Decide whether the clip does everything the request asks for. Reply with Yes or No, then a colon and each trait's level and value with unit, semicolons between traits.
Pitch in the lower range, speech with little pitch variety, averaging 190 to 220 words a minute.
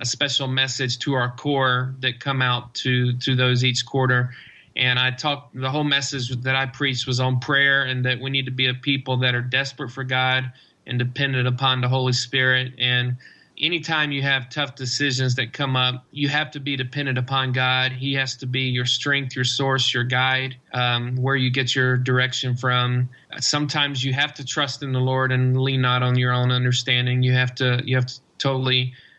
Yes: low, 130 Hz; narrow, 1.4 semitones; fast, 205 wpm